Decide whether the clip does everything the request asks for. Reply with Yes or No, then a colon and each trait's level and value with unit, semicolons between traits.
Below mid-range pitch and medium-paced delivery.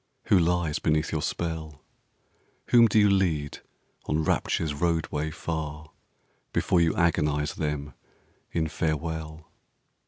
No: very low, 80 Hz; slow, 115 wpm